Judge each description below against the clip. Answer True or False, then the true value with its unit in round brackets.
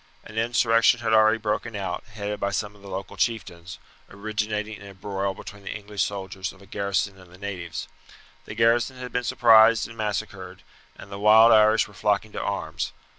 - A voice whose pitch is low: True (105 Hz)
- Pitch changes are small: True (1.9 semitones)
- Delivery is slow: False (190 wpm)